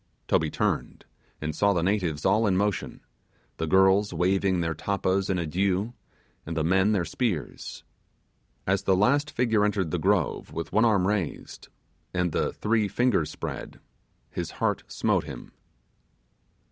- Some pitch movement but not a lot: Yes, average, 3.2 semitones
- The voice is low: Yes, very low, 95 Hz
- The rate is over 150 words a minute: No, average, 145 wpm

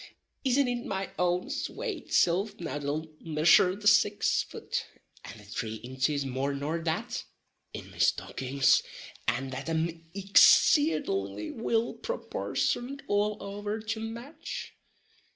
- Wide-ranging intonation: Yes, wide, 7.8 semitones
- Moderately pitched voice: Yes, medium, 180 Hz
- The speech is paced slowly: Yes, slow, 125 wpm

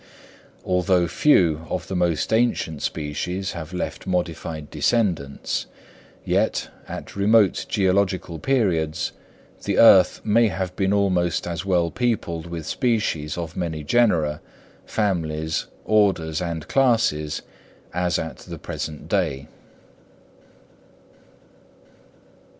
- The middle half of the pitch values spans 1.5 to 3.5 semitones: No, average, 3.9 semitones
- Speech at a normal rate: No, slow, 105 wpm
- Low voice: Yes, very low, 90 Hz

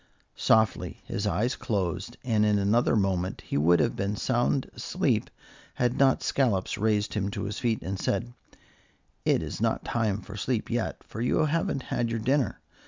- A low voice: Yes, low, 110 Hz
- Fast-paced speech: No, average, 170 wpm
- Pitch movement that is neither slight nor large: Yes, average, 3.6 semitones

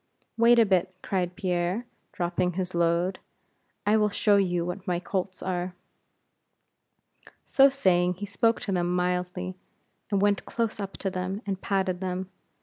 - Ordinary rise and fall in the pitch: No, narrow, 2.1 semitones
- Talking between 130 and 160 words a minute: Yes, average, 150 wpm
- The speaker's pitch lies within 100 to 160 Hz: No, medium, 185 Hz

